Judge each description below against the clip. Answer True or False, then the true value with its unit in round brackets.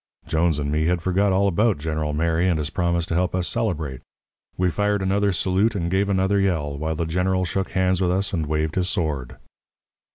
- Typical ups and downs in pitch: True (3.2 semitones)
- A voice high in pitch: False (90 Hz)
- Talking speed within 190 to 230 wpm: True (205 wpm)